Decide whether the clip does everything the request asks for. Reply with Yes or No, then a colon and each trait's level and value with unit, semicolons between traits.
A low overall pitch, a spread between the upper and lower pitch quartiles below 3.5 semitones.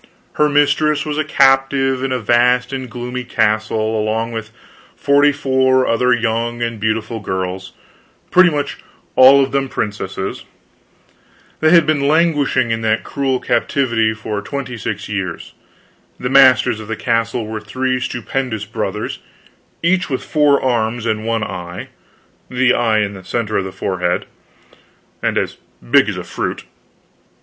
No: low, 120 Hz; average, 3.8 semitones